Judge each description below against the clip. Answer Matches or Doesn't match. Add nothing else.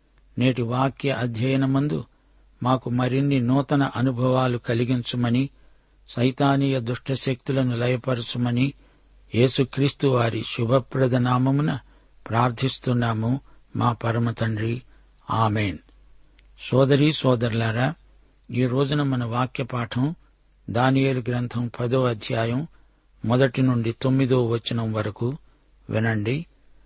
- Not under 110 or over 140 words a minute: Doesn't match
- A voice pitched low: Matches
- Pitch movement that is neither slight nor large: Doesn't match